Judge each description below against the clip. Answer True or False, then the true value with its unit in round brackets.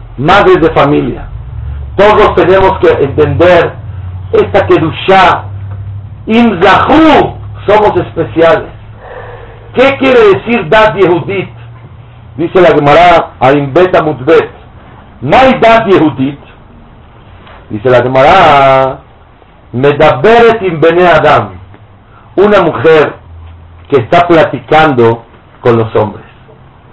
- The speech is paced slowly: True (85 wpm)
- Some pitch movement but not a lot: False (8.1 semitones)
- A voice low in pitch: False (145 Hz)